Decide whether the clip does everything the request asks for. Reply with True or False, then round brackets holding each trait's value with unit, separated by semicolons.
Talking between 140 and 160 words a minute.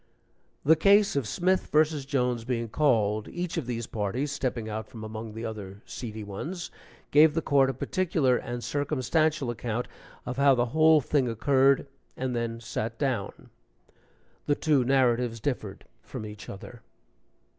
True (155 wpm)